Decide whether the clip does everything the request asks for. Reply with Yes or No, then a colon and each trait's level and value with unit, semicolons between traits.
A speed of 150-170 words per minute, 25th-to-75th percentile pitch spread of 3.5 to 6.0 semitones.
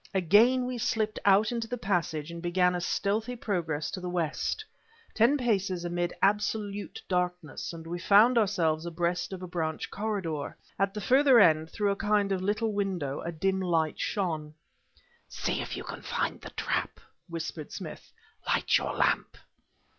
Yes: average, 165 wpm; average, 3.8 semitones